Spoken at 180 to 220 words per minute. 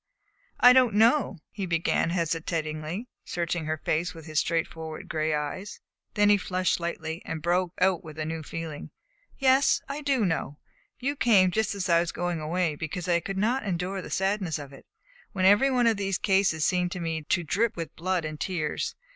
Yes: average, 190 wpm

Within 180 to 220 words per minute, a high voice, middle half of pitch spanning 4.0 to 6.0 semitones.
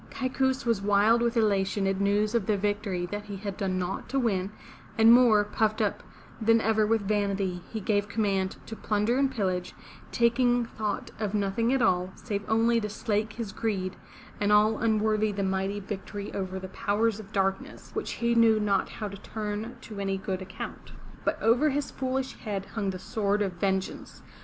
No: average, 185 wpm; high, 210 Hz; narrow, 2.5 semitones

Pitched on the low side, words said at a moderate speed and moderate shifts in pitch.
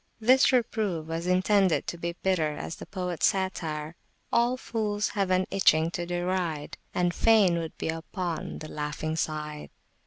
No: medium, 175 Hz; average, 160 wpm; average, 3.5 semitones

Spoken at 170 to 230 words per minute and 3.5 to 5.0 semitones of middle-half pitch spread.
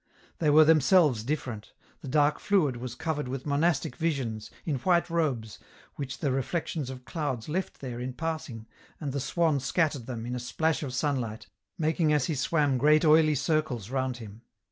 Yes: average, 175 wpm; average, 3.9 semitones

